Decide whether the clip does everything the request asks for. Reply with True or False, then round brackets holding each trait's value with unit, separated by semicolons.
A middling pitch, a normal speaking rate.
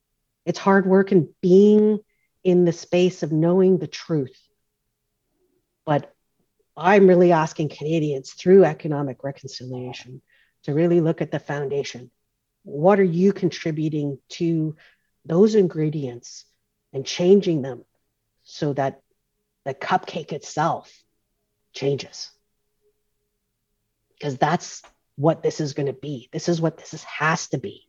False (155 Hz; 125 wpm)